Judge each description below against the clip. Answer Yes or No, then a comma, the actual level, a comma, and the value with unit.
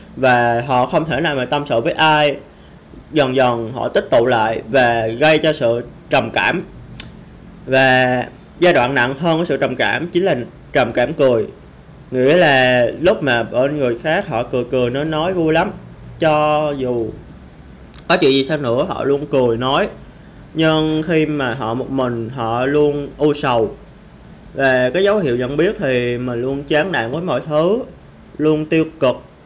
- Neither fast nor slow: Yes, average, 180 wpm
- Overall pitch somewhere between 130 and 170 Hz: Yes, low, 135 Hz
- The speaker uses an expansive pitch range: No, average, 3.9 semitones